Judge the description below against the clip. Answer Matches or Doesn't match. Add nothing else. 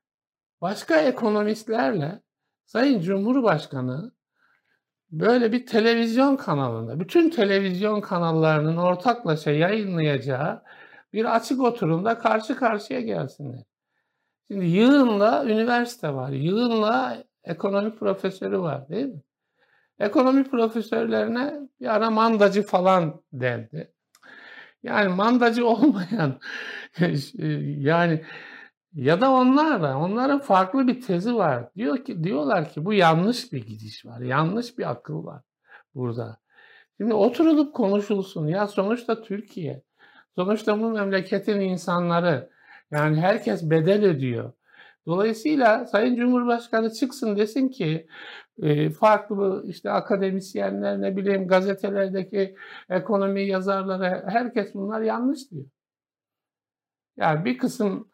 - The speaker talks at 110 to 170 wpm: Doesn't match